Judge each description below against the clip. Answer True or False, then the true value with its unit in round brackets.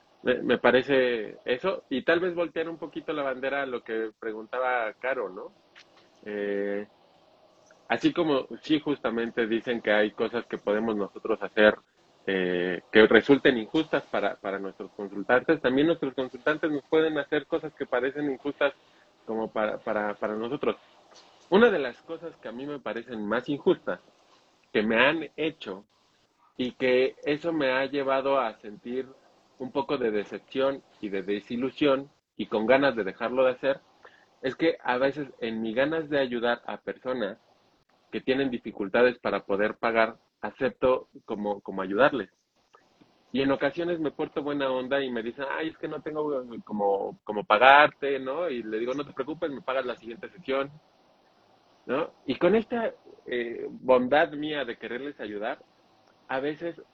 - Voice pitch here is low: True (130 Hz)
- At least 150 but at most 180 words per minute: True (160 wpm)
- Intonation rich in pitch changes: False (4.8 semitones)